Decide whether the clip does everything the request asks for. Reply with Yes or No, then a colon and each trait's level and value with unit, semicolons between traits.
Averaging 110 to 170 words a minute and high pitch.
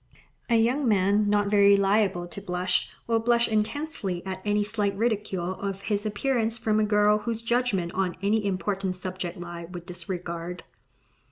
Yes: average, 160 wpm; high, 205 Hz